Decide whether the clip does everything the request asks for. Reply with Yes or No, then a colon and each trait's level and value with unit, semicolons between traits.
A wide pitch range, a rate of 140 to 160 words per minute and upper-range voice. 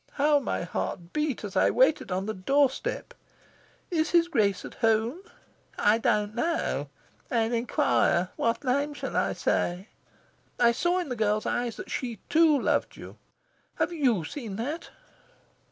Yes: wide, 5.8 semitones; average, 155 wpm; high, 240 Hz